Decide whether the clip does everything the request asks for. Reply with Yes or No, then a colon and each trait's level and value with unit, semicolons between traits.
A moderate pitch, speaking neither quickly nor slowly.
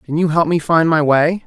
No: medium, 160 Hz; fast, 285 wpm